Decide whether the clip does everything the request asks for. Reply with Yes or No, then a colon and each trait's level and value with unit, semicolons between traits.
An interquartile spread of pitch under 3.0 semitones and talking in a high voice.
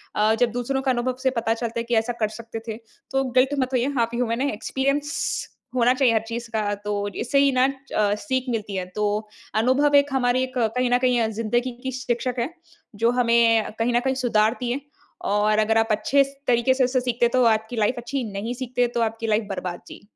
Yes: narrow, 2.5 semitones; high, 240 Hz